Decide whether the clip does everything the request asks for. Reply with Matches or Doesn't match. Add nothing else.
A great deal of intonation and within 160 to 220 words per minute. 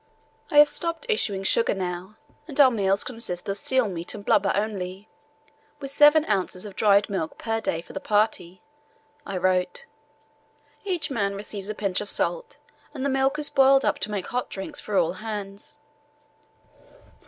Matches